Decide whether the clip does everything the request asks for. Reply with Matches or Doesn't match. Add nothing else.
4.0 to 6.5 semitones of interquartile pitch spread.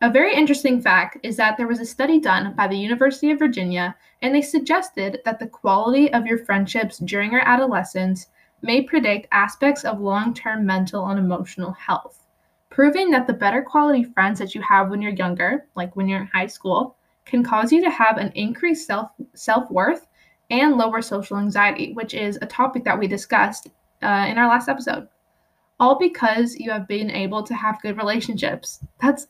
Matches